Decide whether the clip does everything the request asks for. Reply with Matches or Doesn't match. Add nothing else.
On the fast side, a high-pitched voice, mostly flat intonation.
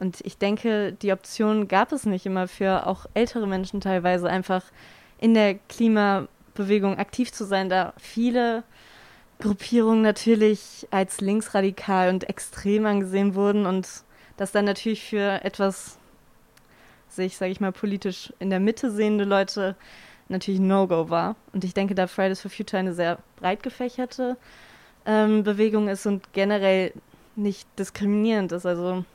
Doesn't match